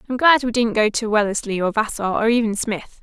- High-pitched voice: Yes, high, 220 Hz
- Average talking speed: No, fast, 240 wpm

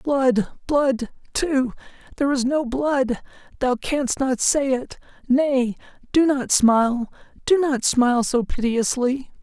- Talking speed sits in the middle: No, slow, 100 wpm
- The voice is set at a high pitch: Yes, very high, 260 Hz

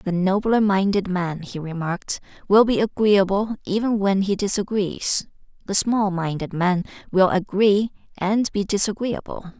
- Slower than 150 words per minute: Yes, average, 140 wpm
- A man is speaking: No, female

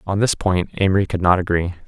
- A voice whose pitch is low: Yes, very low, 90 Hz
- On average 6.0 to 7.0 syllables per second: Yes, 6.1 syllables/s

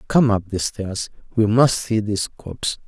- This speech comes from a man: Yes, male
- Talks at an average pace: Yes, average, 190 wpm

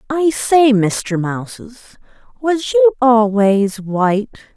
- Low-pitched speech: No, high, 235 Hz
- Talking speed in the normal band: No, slow, 105 wpm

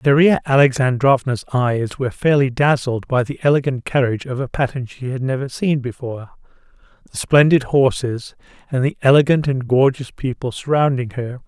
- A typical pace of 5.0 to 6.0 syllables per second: Yes, 5.3 syllables/s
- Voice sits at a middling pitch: No, low, 130 Hz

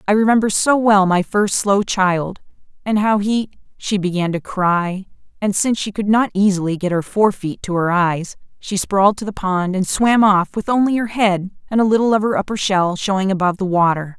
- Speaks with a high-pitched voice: Yes, high, 195 Hz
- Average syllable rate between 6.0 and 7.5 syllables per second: No, 5.3 syllables/s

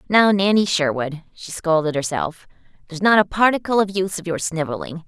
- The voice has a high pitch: No, medium, 180 Hz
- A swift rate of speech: No, average, 175 wpm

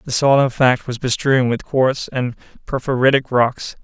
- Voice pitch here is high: No, low, 130 Hz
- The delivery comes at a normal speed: Yes, average, 170 wpm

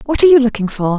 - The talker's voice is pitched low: No, high, 245 Hz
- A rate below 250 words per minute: No, fast, 305 wpm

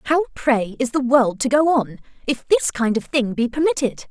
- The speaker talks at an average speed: No, fast, 220 wpm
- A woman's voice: Yes, female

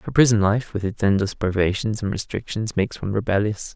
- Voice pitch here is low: Yes, low, 105 Hz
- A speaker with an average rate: Yes, average, 190 wpm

